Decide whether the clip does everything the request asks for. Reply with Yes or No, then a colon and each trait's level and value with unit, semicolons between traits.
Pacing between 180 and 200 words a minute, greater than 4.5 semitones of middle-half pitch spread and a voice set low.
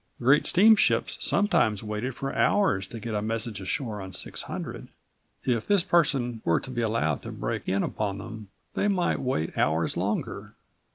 No: average, 165 wpm; average, 5.2 semitones; low, 115 Hz